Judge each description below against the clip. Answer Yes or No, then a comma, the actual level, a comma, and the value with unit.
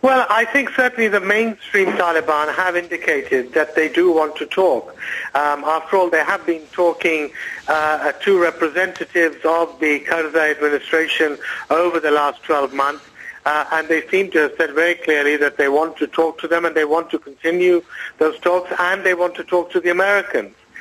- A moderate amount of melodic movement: Yes, average, 3.0 semitones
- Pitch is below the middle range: No, medium, 165 Hz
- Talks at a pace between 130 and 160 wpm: No, average, 185 wpm